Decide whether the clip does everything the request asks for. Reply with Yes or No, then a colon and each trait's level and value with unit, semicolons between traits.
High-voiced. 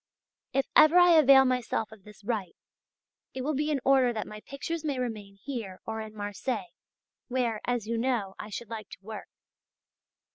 Yes: high, 235 Hz